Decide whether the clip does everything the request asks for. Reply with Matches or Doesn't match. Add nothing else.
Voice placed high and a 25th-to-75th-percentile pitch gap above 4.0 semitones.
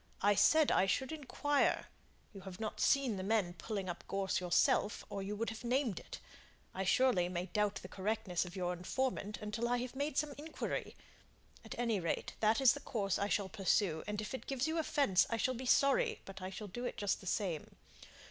Matches